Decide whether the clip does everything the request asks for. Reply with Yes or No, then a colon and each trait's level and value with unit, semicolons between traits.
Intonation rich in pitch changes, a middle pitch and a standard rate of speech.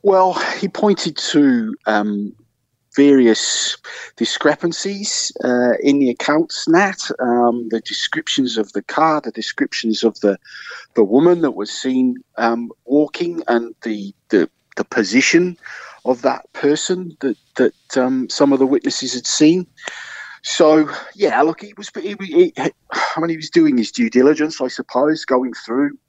Yes: wide, 7.0 semitones; medium, 145 Hz; average, 150 wpm